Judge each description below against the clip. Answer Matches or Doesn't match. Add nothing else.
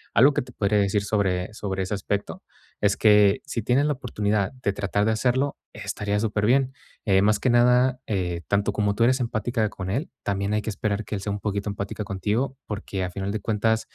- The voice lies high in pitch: Doesn't match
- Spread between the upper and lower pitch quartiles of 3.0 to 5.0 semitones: Doesn't match